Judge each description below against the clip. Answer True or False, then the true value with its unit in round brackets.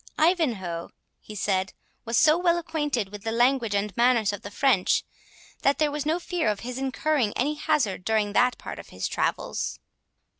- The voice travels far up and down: True (6.4 semitones)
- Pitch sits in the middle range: False (245 Hz)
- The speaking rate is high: False (180 wpm)